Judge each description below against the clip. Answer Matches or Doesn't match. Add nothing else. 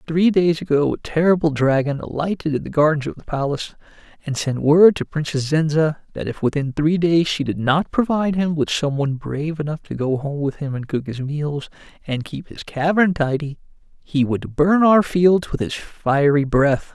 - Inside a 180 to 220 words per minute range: Matches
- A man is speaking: Matches